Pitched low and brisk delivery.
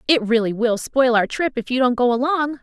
No: very high, 250 Hz; fast, 250 wpm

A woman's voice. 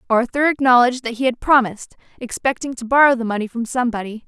Yes: female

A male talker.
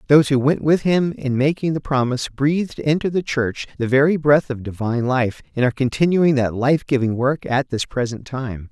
Yes: male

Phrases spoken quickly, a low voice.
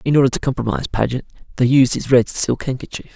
Yes: fast, 210 wpm; low, 130 Hz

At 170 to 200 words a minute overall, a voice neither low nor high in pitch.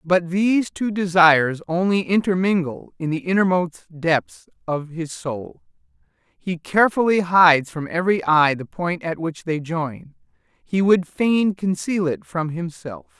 No: average, 145 wpm; medium, 175 Hz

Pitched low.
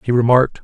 Yes: low, 125 Hz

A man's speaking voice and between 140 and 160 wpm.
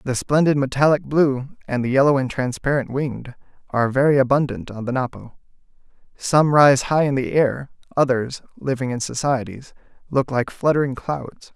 Yes: male; average, 155 wpm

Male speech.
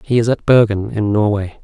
Yes: male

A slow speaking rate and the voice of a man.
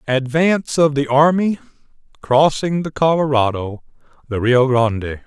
Yes: slow, 90 wpm; male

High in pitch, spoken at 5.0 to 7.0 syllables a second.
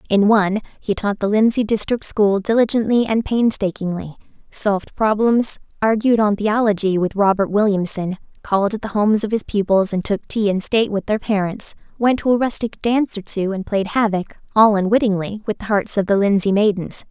Yes: high, 210 Hz; 5.4 syllables/s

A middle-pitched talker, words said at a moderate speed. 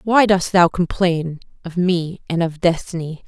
Yes: medium, 175 Hz; average, 165 wpm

